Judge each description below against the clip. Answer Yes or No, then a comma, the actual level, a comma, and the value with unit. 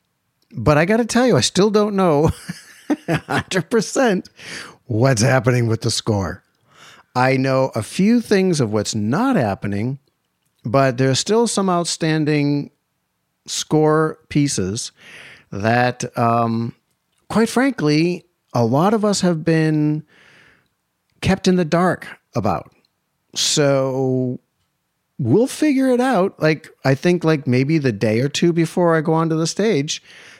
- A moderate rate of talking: No, slow, 130 wpm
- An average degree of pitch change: No, wide, 6.2 semitones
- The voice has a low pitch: No, medium, 150 Hz